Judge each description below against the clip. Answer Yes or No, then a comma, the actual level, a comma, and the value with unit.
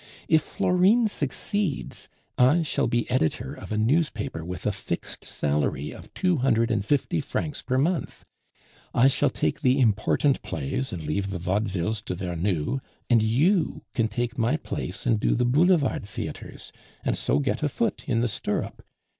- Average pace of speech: Yes, average, 165 wpm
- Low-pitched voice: Yes, low, 120 Hz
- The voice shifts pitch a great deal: Yes, wide, 6.6 semitones